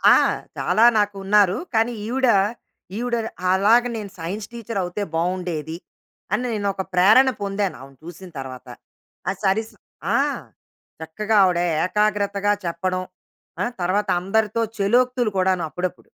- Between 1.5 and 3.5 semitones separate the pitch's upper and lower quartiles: Yes, average, 3.2 semitones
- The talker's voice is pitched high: Yes, high, 200 Hz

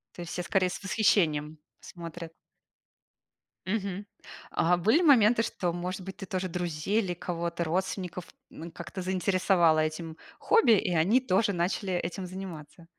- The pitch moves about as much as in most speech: No, narrow, 2.3 semitones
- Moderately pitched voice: Yes, medium, 180 Hz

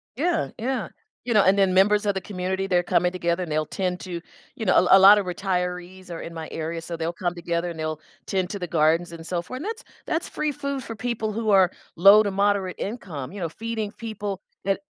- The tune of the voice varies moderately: Yes, average, 3.4 semitones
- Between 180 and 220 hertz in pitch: Yes, high, 190 Hz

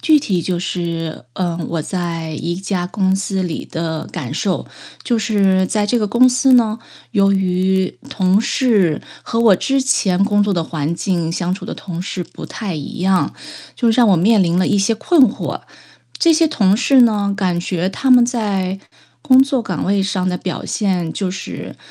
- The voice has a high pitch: Yes, high, 195 Hz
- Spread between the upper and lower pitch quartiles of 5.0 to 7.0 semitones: No, average, 3.9 semitones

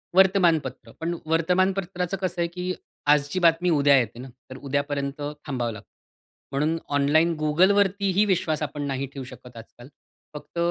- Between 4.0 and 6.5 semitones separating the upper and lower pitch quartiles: Yes, average, 4.5 semitones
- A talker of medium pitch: Yes, medium, 155 Hz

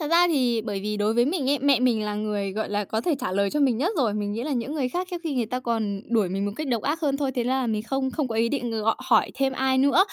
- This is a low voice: No, high, 245 Hz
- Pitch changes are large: No, average, 4.5 semitones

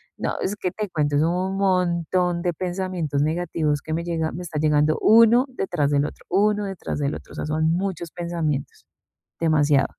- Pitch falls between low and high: Yes, medium, 170 Hz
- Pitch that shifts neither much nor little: Yes, average, 3.5 semitones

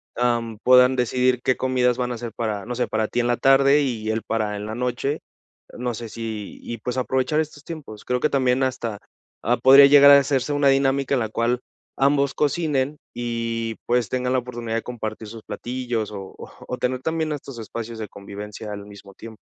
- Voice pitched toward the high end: No, low, 125 Hz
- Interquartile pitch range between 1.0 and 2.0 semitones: No, average, 2.8 semitones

